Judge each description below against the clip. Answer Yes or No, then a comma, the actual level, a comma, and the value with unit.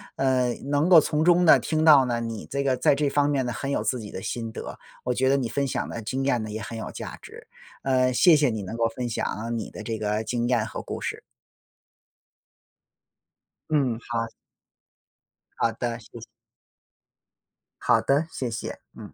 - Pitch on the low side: Yes, low, 125 Hz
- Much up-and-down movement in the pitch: No, average, 3.4 semitones